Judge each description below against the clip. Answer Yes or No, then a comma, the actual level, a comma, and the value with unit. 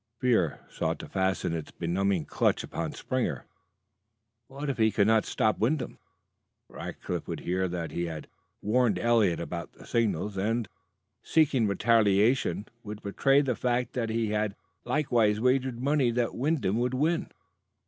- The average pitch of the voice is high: No, low, 110 Hz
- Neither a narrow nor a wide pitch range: Yes, average, 4.3 semitones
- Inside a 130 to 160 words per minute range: Yes, average, 150 wpm